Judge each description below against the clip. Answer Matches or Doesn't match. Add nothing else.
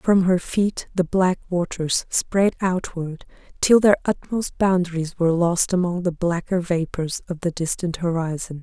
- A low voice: Doesn't match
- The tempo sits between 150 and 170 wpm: Matches